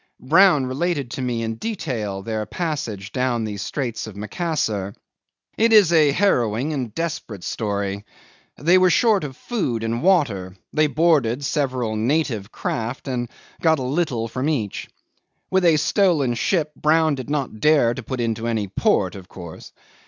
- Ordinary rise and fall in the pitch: No, wide, 6.1 semitones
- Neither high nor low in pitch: No, low, 130 Hz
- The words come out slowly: No, average, 160 wpm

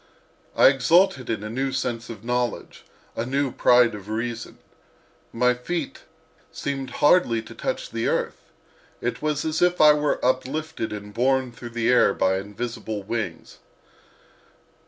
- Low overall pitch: Yes, low, 125 Hz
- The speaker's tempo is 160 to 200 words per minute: No, average, 145 wpm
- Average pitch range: Yes, average, 4.0 semitones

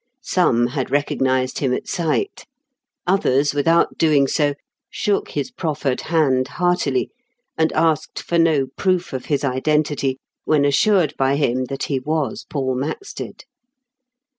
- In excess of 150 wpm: No, slow, 135 wpm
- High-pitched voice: No, medium, 145 Hz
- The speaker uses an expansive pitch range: No, average, 3.7 semitones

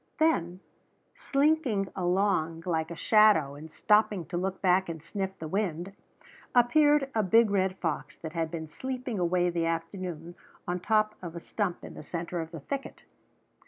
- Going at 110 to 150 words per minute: No, average, 165 wpm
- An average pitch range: Yes, average, 4.3 semitones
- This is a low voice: No, medium, 180 Hz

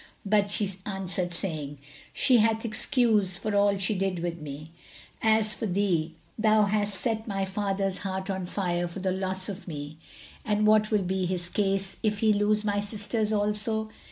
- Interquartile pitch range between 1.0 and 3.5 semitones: Yes, narrow, 2.4 semitones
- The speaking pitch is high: Yes, high, 200 Hz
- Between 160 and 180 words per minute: Yes, average, 175 wpm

